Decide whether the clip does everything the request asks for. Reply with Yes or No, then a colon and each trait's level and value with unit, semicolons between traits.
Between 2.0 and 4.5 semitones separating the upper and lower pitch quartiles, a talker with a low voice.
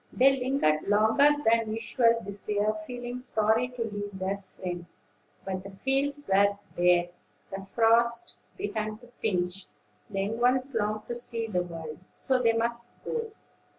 No: average, 3.8 semitones; high, 220 Hz